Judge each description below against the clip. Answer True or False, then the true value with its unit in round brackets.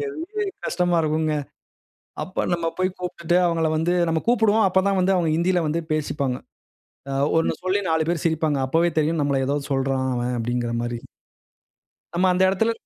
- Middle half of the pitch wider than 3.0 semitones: True (4.2 semitones)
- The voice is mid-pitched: True (165 Hz)